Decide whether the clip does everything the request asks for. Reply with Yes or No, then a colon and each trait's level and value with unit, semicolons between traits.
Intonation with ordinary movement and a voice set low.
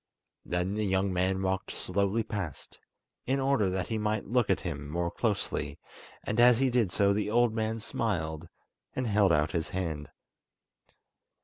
Yes: average, 3.9 semitones; low, 100 Hz